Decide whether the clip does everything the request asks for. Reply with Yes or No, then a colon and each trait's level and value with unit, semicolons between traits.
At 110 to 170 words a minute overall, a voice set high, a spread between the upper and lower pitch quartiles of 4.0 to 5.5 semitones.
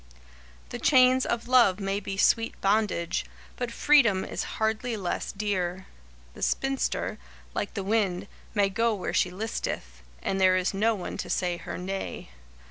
No: average, 155 wpm; high, 200 Hz; average, 3.4 semitones